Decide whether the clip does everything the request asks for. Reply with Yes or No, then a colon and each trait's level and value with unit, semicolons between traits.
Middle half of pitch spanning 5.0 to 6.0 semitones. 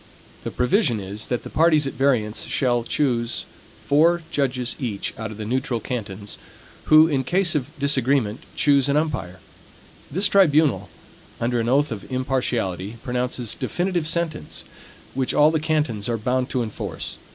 No: average, 4.5 semitones